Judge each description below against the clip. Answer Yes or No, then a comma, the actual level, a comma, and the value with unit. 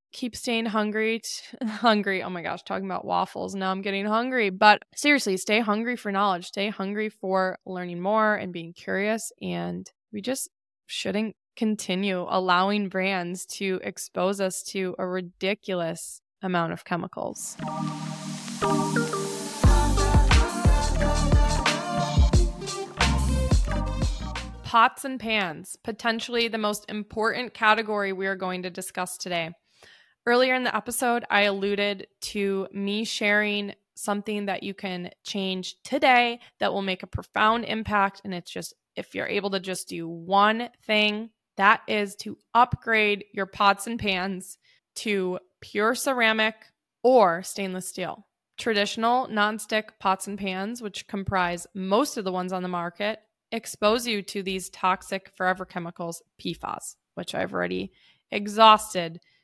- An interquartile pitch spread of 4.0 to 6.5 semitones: No, average, 2.9 semitones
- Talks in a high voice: Yes, high, 200 Hz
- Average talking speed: No, slow, 130 wpm